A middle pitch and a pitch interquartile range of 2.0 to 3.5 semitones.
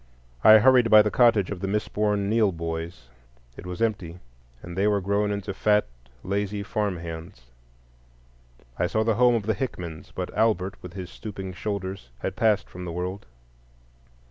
No: low, 100 Hz; average, 2.9 semitones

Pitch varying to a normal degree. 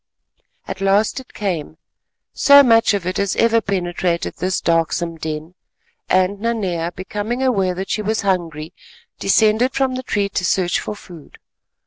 Yes: average, 4.0 semitones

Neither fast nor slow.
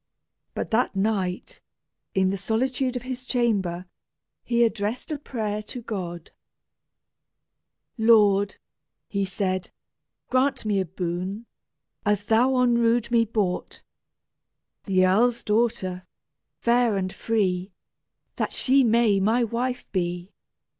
No: slow, 115 wpm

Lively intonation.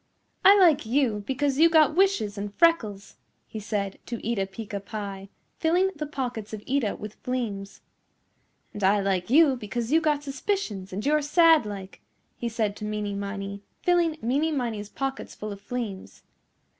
Yes: wide, 6.4 semitones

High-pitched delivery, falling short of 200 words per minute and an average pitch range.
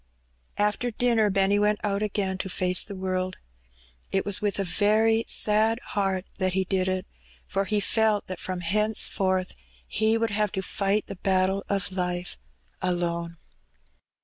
No: high, 195 Hz; average, 155 wpm; narrow, 2.1 semitones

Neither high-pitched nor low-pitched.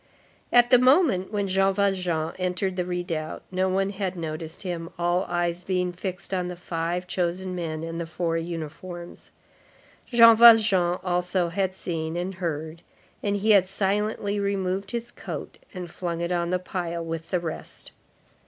Yes: medium, 180 Hz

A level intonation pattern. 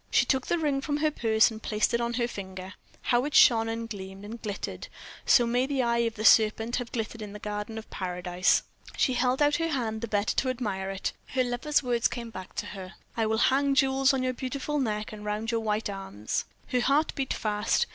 No: average, 3.6 semitones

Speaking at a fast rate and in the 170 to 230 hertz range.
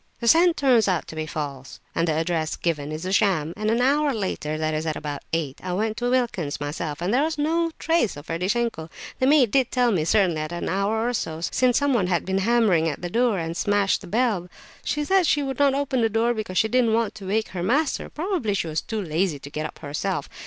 Yes: fast, 240 wpm; high, 200 Hz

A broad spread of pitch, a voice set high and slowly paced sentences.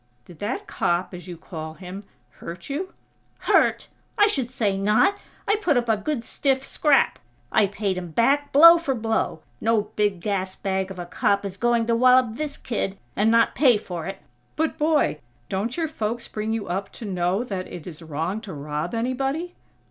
No: wide, 5.9 semitones; high, 215 Hz; average, 190 wpm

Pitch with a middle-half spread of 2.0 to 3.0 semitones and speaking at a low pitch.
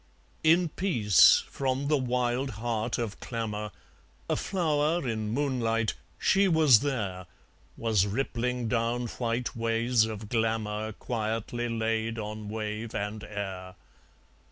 Yes: average, 2.7 semitones; low, 115 Hz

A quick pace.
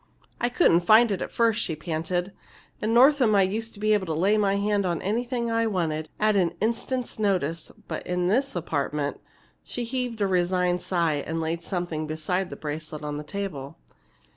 No: average, 190 wpm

